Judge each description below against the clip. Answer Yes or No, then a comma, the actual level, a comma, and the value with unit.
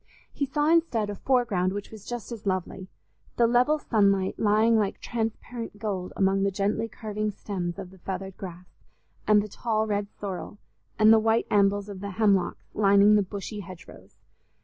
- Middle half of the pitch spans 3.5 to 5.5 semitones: No, narrow, 2.4 semitones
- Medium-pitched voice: No, high, 205 Hz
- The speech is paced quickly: No, average, 170 wpm